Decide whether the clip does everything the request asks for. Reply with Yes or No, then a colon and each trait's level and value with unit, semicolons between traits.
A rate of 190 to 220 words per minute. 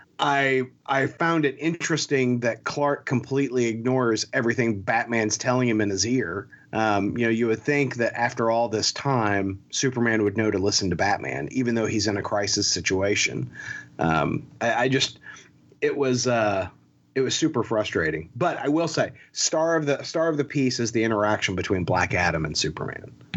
No: average, 180 wpm